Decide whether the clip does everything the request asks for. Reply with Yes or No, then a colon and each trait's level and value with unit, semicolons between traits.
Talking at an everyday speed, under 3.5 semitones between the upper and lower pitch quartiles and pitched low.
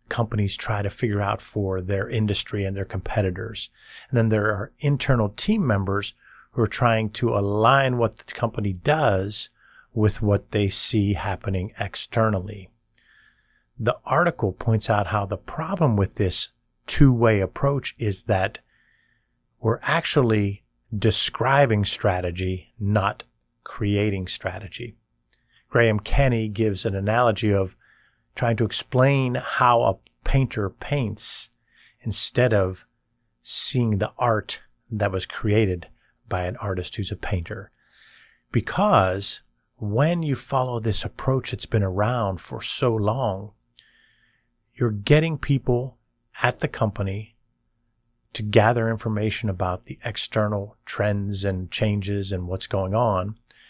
No: slow, 125 wpm; average, 2.9 semitones; low, 110 Hz